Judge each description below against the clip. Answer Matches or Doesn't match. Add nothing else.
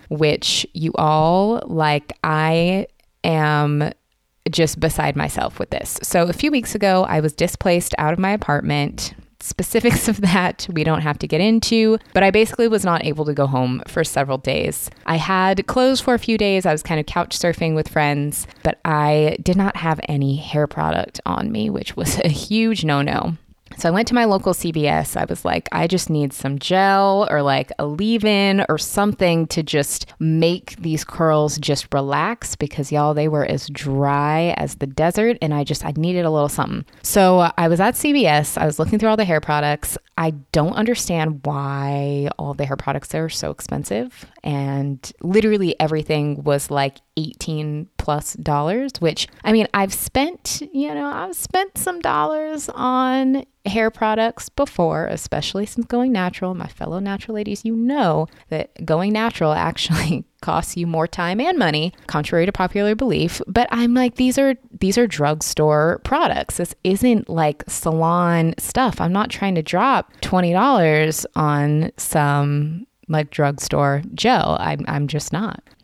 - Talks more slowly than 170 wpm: Doesn't match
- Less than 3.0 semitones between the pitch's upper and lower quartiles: Doesn't match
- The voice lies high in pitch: Doesn't match